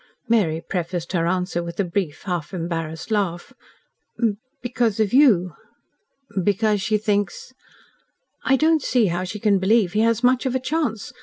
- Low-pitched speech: No, high, 200 Hz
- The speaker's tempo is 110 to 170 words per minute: Yes, average, 160 wpm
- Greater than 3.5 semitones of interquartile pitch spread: Yes, average, 4.8 semitones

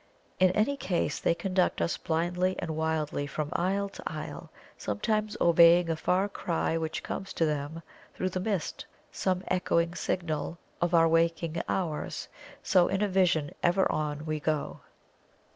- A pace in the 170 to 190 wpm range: No, average, 155 wpm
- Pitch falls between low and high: Yes, medium, 170 Hz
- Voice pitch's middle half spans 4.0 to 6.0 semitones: No, average, 2.7 semitones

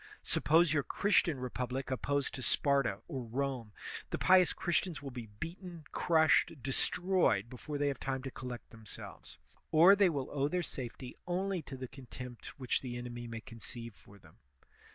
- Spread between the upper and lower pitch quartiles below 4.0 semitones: No, average, 5.1 semitones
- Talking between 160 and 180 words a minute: Yes, average, 165 wpm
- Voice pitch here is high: No, low, 135 Hz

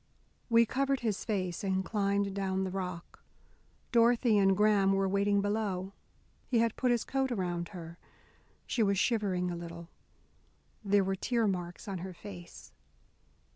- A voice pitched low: No, high, 195 Hz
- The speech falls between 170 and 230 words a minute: No, average, 150 wpm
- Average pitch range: Yes, average, 3.0 semitones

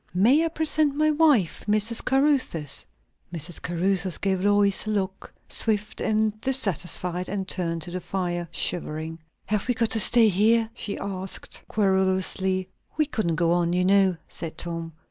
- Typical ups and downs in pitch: Yes, average, 4.0 semitones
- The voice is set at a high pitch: Yes, high, 195 Hz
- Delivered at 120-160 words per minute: Yes, average, 155 wpm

